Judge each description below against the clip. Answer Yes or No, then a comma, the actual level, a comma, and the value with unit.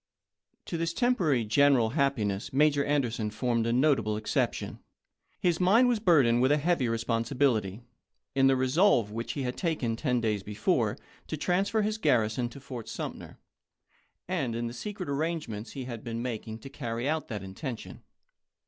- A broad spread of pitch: No, average, 4.9 semitones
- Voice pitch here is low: Yes, low, 130 Hz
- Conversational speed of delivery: Yes, average, 170 wpm